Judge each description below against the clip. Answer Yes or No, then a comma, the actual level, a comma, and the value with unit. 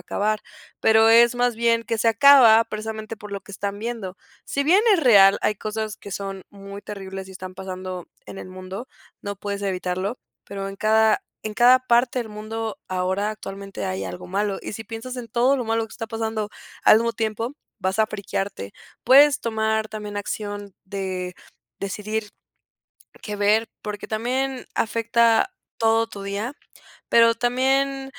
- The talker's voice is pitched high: Yes, high, 215 Hz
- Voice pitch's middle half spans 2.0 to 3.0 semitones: Yes, narrow, 2.6 semitones